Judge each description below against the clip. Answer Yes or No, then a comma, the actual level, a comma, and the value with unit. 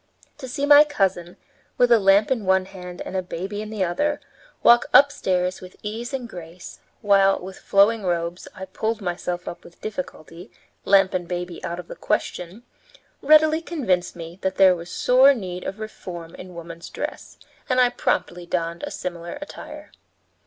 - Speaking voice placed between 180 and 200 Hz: Yes, high, 190 Hz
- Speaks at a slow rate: No, average, 175 wpm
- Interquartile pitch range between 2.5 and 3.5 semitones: No, average, 4.3 semitones